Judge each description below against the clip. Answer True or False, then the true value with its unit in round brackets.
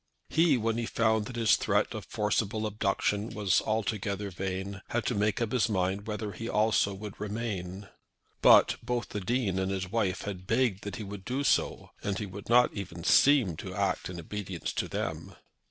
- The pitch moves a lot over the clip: False (2.9 semitones)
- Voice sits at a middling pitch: False (105 Hz)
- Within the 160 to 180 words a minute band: False (190 wpm)